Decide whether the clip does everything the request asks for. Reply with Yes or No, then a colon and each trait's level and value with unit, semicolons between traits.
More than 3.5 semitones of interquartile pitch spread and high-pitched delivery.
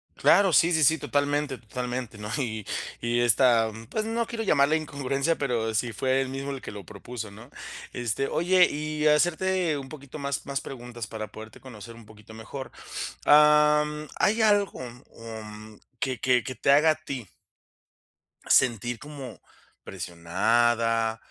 No: average, 4.6 semitones; low, 130 Hz